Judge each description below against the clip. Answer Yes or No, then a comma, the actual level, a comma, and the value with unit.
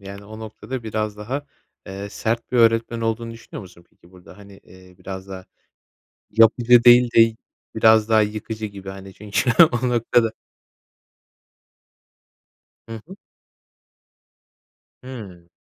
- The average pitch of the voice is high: No, low, 110 Hz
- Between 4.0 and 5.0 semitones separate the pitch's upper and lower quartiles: No, average, 2.9 semitones